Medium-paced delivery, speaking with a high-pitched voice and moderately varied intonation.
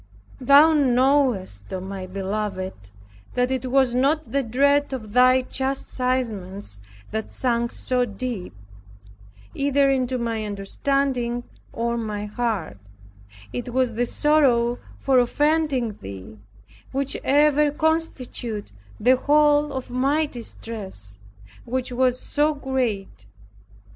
No: slow, 110 wpm; very high, 250 Hz; average, 4.4 semitones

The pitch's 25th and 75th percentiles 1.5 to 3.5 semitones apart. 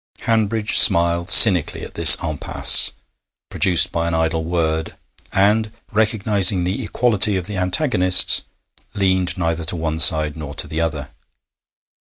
No: average, 4.1 semitones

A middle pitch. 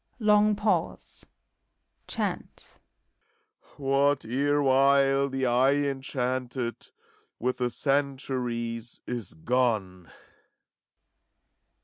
No: low, 130 Hz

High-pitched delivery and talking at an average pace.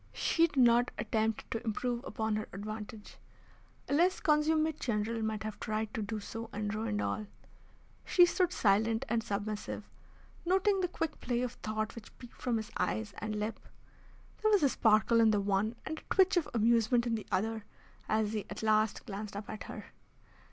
Yes: high, 220 Hz; average, 185 wpm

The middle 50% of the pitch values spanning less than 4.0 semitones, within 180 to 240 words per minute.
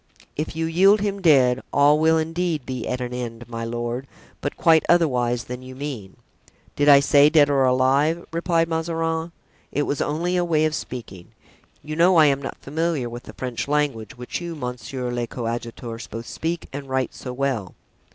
No: average, 4.6 semitones; average, 185 wpm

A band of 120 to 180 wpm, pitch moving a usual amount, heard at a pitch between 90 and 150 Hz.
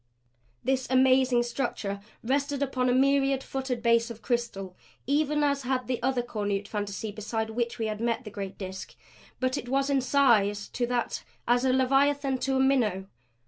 No: average, 175 wpm; average, 3.3 semitones; very high, 250 Hz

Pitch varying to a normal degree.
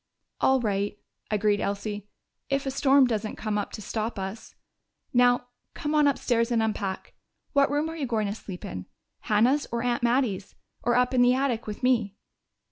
Yes: average, 3.9 semitones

